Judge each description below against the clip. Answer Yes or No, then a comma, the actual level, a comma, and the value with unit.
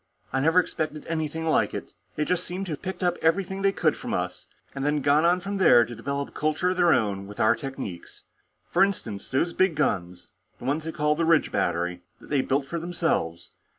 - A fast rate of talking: Yes, fast, 220 wpm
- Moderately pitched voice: Yes, medium, 150 Hz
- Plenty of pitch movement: No, average, 4.8 semitones